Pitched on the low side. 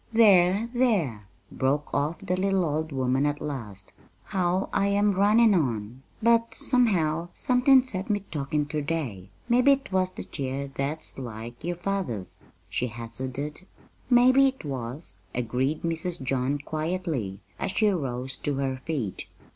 No: medium, 155 Hz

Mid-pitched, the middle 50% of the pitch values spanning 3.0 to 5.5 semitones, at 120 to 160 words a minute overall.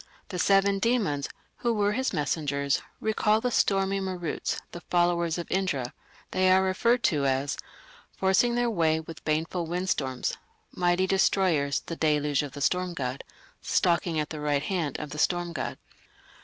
Yes: medium, 175 Hz; average, 4.5 semitones; average, 155 wpm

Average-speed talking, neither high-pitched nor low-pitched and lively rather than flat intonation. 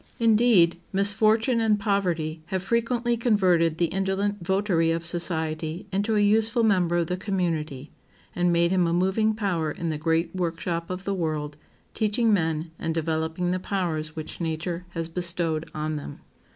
No: average, 160 wpm; medium, 175 Hz; average, 3.8 semitones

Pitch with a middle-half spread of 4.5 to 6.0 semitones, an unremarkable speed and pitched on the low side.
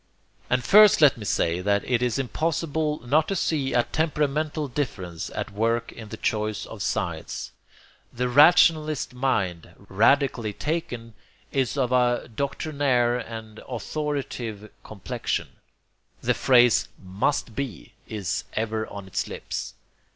No: average, 5.0 semitones; slow, 130 wpm; low, 125 Hz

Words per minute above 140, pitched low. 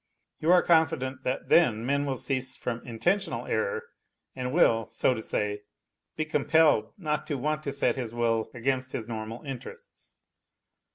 Yes: average, 160 wpm; low, 130 Hz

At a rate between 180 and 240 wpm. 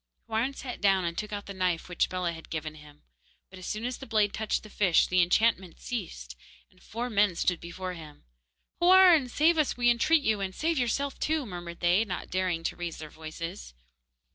Yes: fast, 205 wpm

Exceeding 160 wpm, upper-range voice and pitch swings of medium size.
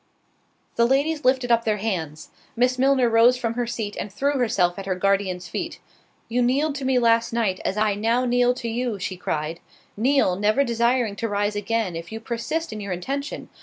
Yes: average, 190 wpm; high, 230 Hz; average, 3.8 semitones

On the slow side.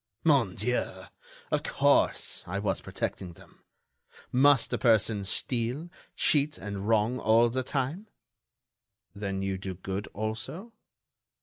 Yes: slow, 120 wpm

